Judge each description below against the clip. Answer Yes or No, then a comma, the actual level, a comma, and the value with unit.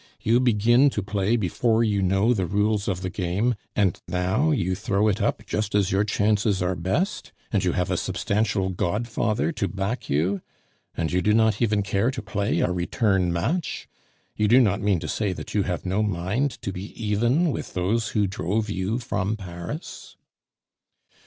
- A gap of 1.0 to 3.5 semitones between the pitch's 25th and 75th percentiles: Yes, average, 3.1 semitones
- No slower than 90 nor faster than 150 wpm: No, average, 185 wpm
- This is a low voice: Yes, low, 105 Hz